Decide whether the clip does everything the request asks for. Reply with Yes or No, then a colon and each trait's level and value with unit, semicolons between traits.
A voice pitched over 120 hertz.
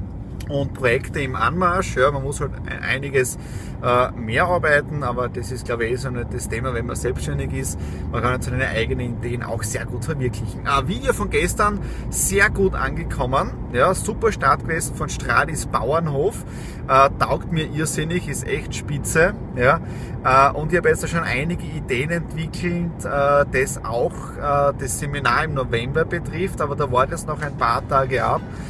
Yes: low, 135 Hz